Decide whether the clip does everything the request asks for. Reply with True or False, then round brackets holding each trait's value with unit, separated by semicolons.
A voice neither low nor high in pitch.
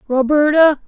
False (290 Hz)